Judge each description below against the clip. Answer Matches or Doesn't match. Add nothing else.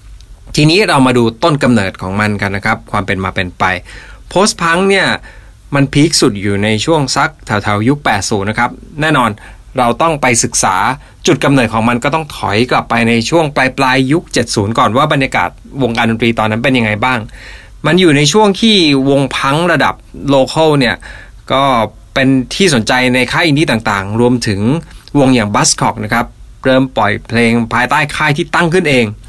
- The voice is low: Matches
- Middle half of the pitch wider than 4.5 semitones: Matches